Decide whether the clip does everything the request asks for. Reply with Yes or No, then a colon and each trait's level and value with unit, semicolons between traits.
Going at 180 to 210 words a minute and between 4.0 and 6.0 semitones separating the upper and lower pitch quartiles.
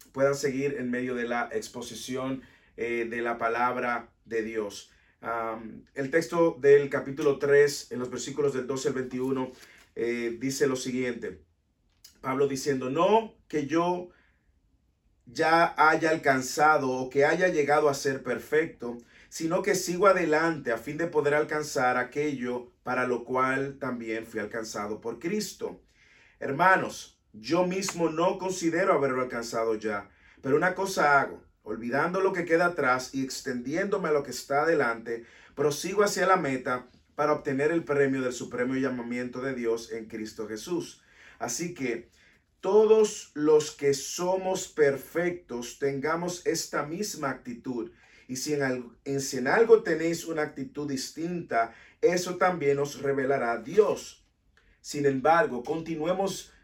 No: average, 140 wpm; average, 5.1 semitones